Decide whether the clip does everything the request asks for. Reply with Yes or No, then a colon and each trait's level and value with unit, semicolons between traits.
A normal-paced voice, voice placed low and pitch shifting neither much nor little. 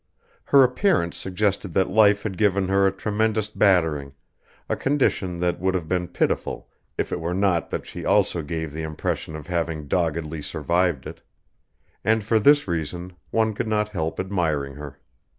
Yes: average, 170 wpm; very low, 90 Hz; average, 4.4 semitones